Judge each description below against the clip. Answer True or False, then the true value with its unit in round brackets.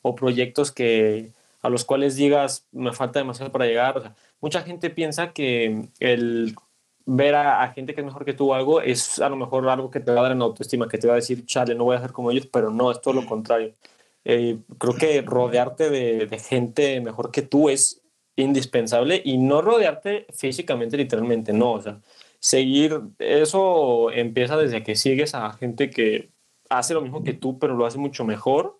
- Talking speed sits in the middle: False (205 wpm)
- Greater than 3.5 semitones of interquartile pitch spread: False (3.1 semitones)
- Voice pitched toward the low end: True (130 Hz)